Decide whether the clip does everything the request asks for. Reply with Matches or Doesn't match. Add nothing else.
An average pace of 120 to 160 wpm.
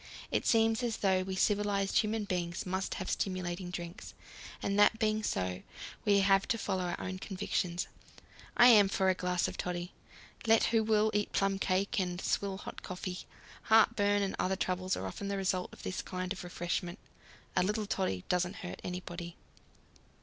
Doesn't match